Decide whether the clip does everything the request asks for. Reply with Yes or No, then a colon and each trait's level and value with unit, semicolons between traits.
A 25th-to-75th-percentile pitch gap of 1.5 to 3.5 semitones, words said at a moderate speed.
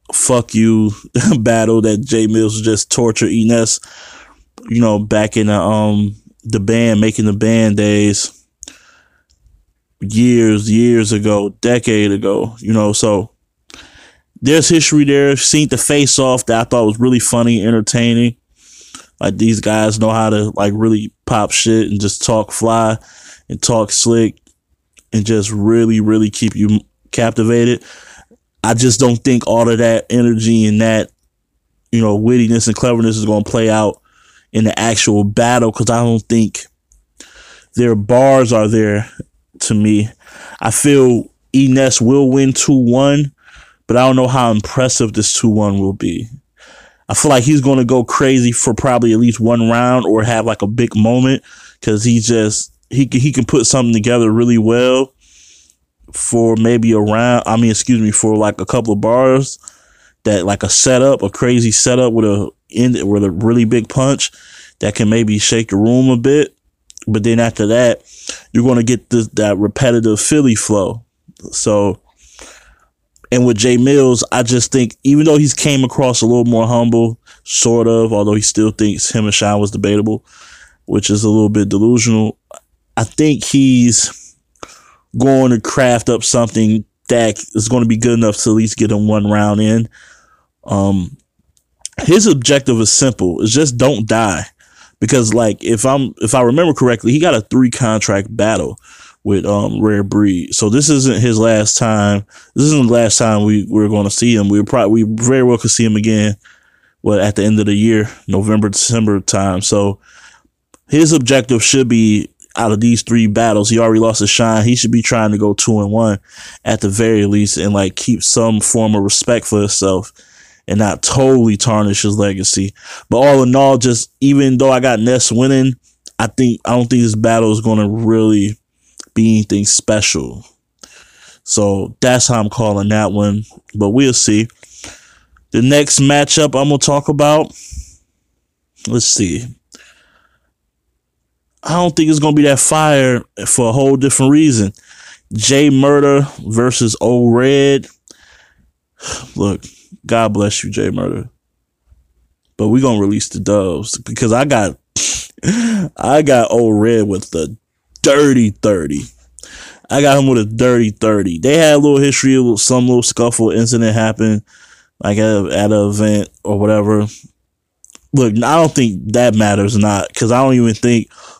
Yes: average, 2.9 semitones; average, 170 wpm